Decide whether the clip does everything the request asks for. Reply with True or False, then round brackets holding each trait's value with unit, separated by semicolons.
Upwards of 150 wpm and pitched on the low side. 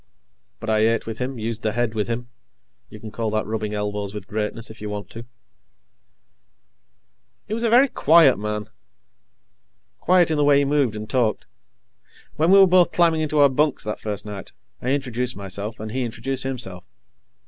True (185 wpm; 115 Hz)